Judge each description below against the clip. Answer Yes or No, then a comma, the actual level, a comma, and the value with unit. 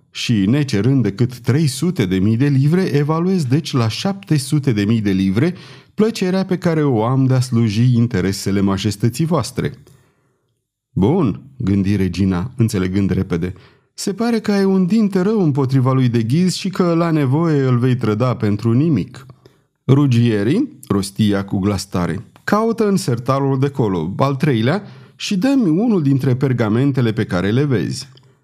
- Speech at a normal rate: Yes, average, 150 wpm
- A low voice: Yes, low, 130 Hz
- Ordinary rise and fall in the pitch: No, wide, 6.4 semitones